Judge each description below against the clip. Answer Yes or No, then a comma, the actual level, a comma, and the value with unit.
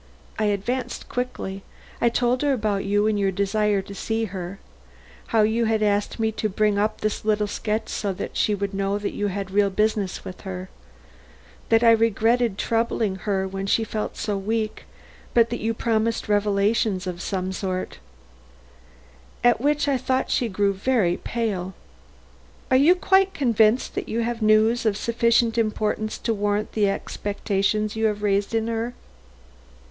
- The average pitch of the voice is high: Yes, high, 215 Hz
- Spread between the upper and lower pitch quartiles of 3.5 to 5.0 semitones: No, narrow, 2.4 semitones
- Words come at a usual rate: Yes, average, 170 wpm